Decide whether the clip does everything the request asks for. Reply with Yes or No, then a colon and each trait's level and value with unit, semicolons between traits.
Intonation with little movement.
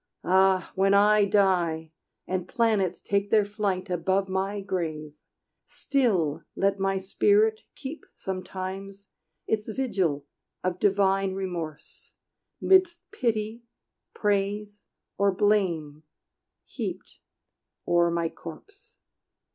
Yes: narrow, 2.2 semitones